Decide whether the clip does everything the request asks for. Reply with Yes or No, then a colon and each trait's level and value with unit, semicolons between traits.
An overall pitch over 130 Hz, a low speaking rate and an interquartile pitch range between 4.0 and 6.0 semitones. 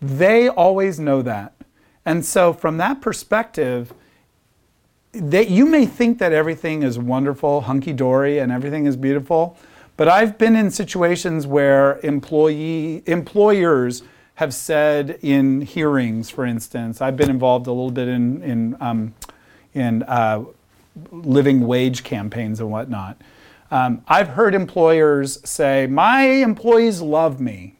Yes: medium, 140 Hz; slow, 130 wpm; average, 5.1 semitones